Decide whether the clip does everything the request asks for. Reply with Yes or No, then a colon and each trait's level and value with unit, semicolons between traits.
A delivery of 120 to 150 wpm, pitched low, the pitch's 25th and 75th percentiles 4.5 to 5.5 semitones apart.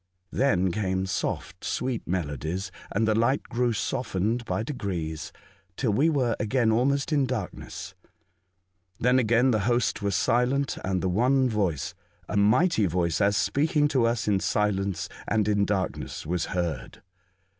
Yes: average, 145 wpm; low, 105 Hz; average, 4.9 semitones